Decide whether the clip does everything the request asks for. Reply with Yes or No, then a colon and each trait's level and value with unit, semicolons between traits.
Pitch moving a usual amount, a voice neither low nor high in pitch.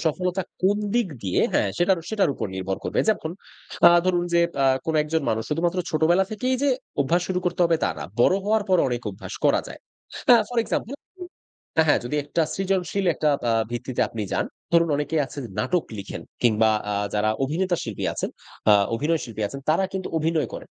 No: wide, 6.1 semitones; medium, 165 Hz